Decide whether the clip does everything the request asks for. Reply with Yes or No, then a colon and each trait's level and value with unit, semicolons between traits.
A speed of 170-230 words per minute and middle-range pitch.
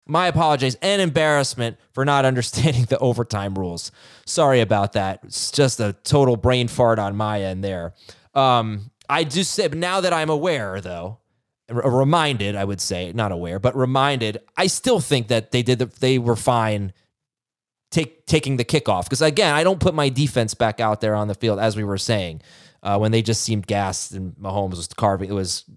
No: average, 195 wpm; low, 120 Hz